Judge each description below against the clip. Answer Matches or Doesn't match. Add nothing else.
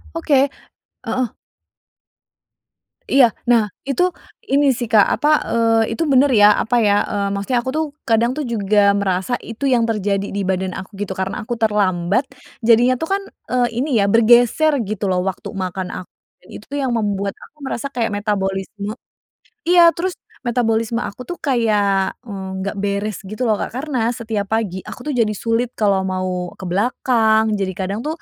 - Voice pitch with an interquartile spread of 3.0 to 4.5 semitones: Matches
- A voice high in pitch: Matches